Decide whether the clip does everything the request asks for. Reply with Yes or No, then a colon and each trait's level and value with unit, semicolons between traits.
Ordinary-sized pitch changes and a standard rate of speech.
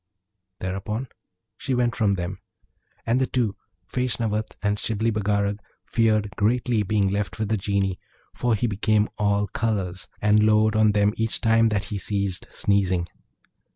No: narrow, 1.9 semitones; average, 150 wpm